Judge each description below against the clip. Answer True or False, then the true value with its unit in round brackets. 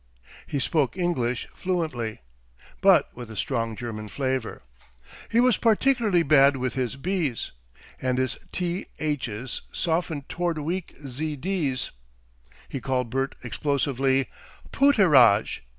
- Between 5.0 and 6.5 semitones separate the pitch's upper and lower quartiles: True (5.4 semitones)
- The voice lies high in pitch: False (135 Hz)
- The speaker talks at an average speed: False (110 wpm)